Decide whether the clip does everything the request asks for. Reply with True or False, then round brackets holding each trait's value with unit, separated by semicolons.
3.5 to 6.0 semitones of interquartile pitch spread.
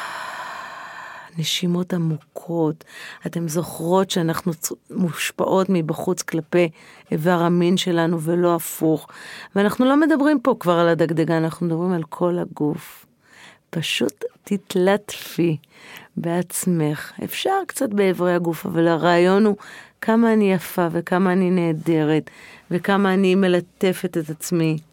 False (2.7 semitones)